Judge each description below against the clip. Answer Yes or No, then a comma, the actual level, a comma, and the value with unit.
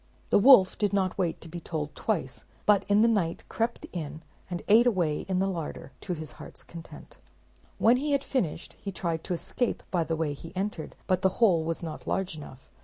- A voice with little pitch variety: No, average, 4.0 semitones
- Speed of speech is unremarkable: No, fast, 210 wpm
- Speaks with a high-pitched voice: No, medium, 180 Hz